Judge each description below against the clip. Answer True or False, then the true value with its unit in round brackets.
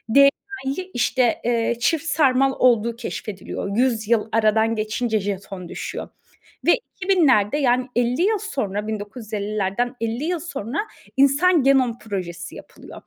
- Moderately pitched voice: False (240 Hz)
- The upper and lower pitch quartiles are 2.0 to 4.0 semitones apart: False (4.5 semitones)